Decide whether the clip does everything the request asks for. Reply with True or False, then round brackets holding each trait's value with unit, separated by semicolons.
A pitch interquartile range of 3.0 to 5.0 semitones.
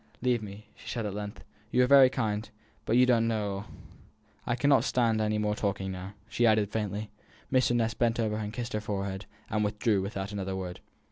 False (2.5 semitones)